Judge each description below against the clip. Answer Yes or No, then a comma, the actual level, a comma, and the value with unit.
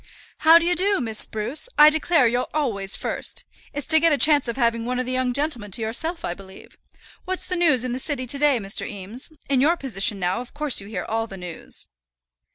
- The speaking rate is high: Yes, fast, 225 wpm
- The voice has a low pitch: No, very high, 255 Hz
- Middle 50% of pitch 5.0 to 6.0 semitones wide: Yes, wide, 5.5 semitones